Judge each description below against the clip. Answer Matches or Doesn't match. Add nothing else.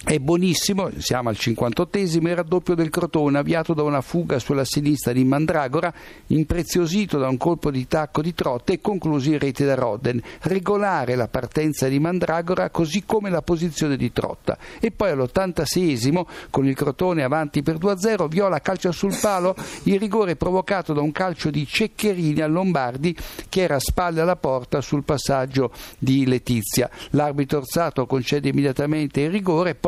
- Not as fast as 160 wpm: Doesn't match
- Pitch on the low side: Doesn't match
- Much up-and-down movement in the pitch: Doesn't match